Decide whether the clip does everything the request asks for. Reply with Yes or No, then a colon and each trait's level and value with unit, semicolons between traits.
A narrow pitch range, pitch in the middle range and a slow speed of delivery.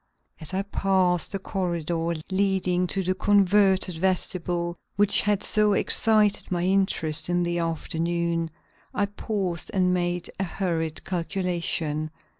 Yes: narrow, 2.3 semitones; medium, 180 Hz; slow, 125 wpm